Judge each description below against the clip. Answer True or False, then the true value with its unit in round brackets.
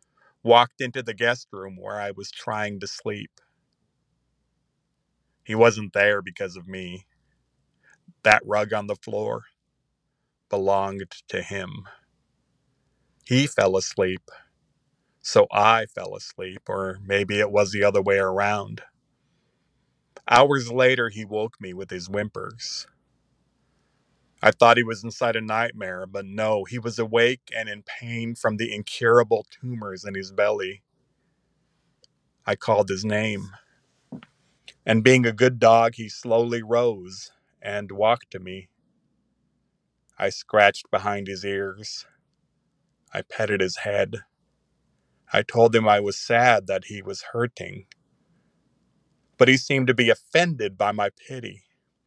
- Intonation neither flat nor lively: True (3.0 semitones)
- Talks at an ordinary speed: False (130 wpm)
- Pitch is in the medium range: False (105 Hz)